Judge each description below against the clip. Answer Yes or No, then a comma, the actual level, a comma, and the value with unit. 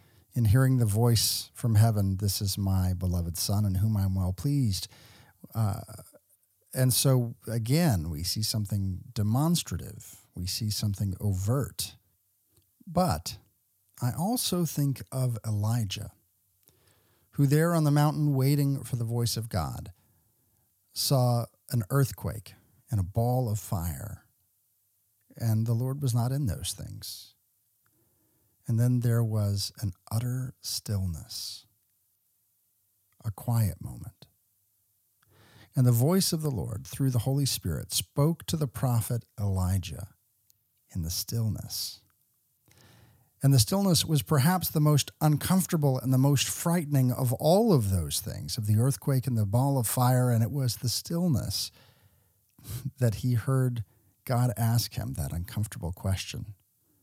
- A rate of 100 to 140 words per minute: Yes, slow, 135 wpm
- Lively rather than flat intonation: No, average, 4.2 semitones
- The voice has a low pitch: Yes, low, 110 Hz